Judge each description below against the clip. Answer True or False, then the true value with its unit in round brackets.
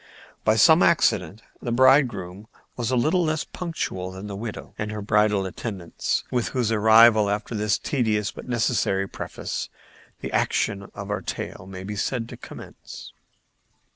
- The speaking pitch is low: True (105 Hz)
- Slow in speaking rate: False (155 wpm)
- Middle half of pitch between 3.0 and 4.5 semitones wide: True (3.5 semitones)